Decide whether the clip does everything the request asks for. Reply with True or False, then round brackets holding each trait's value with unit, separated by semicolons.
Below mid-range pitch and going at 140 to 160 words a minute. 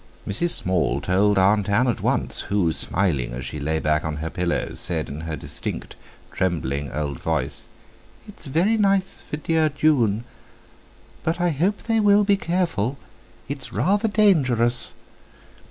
True (115 Hz; 145 wpm)